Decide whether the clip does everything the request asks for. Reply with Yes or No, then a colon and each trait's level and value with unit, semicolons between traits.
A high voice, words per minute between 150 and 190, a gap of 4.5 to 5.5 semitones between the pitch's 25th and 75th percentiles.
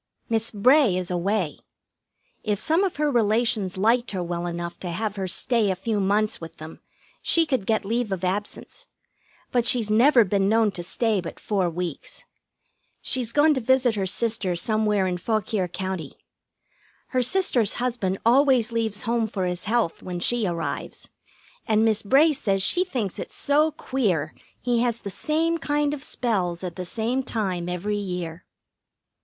Yes: high, 215 Hz; average, 170 wpm; average, 4.8 semitones